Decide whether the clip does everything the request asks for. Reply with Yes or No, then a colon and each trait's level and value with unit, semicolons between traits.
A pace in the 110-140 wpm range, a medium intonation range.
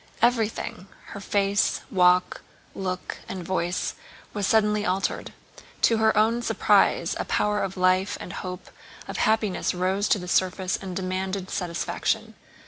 No: slow, 135 wpm; narrow, 2.3 semitones